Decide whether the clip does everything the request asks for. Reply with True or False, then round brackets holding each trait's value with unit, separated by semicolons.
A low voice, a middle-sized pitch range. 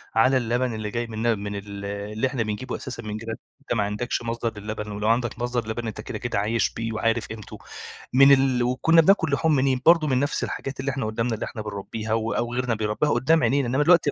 True (115 Hz; 3.3 semitones)